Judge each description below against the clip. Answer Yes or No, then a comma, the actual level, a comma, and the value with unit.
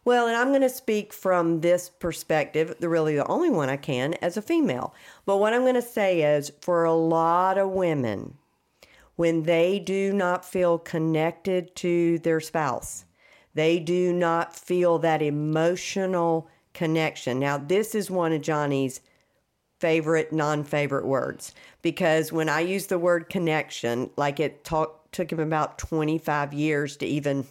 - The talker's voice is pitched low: No, medium, 165 Hz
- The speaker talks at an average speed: Yes, average, 160 wpm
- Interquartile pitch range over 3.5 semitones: No, average, 2.7 semitones